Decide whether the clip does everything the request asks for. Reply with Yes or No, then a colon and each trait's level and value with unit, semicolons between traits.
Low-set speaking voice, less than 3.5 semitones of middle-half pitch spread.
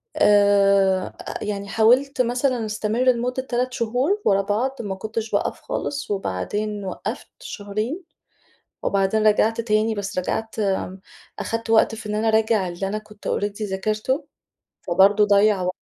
No: high, 215 Hz; narrow, 2.5 semitones